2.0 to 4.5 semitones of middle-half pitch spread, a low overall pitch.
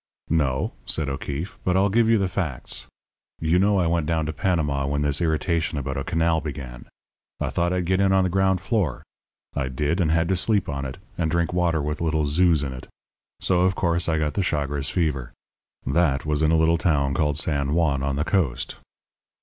Yes: average, 3.8 semitones; very low, 80 Hz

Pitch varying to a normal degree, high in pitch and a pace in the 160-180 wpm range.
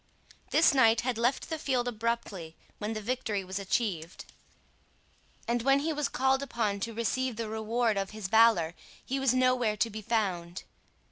Yes: average, 3.7 semitones; high, 230 Hz; average, 165 wpm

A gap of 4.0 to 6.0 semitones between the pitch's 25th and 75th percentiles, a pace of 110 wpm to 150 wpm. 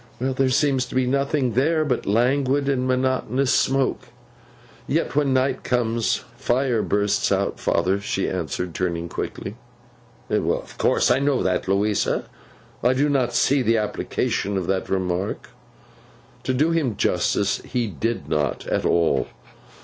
Yes: average, 5.1 semitones; average, 145 wpm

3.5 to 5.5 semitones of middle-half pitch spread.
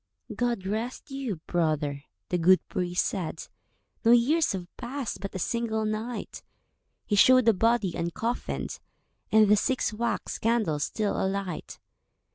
Yes: average, 4.2 semitones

